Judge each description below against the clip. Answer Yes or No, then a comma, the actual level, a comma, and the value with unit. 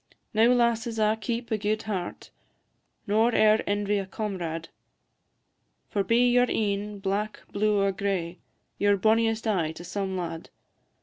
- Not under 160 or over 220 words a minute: No, average, 145 wpm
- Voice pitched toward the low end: No, high, 210 Hz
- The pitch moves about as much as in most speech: No, narrow, 2.3 semitones